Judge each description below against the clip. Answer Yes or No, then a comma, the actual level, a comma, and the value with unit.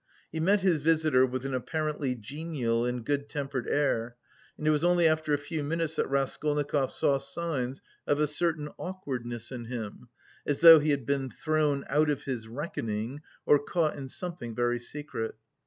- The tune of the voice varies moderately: Yes, average, 3.6 semitones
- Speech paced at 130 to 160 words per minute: No, average, 175 wpm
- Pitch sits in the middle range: Yes, medium, 145 Hz